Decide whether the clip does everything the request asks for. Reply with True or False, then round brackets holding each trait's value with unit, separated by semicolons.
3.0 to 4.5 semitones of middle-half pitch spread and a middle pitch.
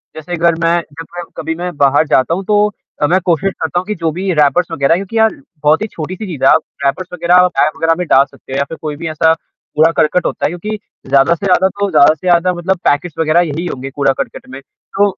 True (3.3 semitones; 165 Hz)